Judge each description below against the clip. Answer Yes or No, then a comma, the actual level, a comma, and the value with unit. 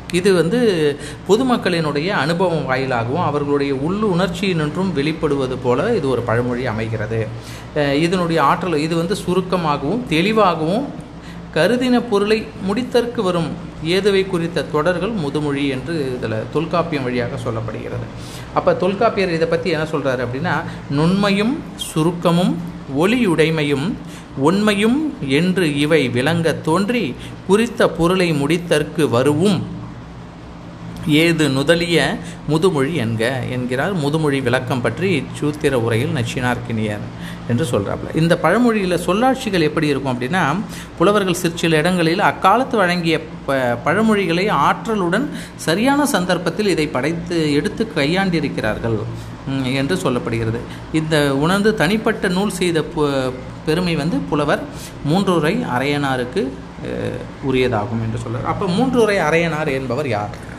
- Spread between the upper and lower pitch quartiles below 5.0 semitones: No, average, 5.3 semitones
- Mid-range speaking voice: Yes, medium, 160 Hz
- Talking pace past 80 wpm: Yes, average, 105 wpm